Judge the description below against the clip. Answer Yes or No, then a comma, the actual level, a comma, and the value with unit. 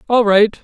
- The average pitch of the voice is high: Yes, high, 220 Hz